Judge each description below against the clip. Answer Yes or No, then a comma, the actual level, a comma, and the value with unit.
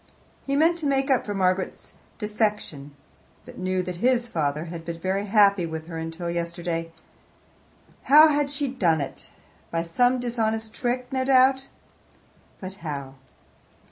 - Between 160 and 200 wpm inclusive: No, average, 145 wpm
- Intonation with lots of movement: Yes, wide, 7.2 semitones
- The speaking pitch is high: Yes, high, 200 Hz